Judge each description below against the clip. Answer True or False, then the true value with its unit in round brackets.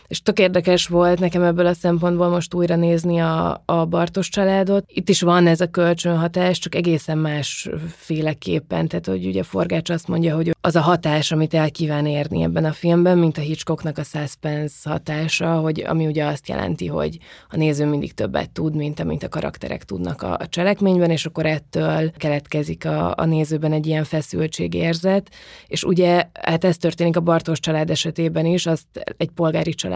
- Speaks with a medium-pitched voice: True (165 Hz)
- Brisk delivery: True (185 wpm)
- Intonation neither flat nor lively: False (2.2 semitones)